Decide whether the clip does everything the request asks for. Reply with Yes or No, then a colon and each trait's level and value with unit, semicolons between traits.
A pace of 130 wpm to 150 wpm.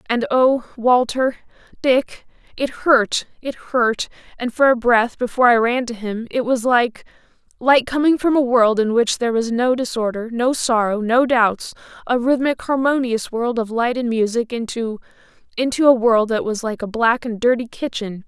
No: average, 160 wpm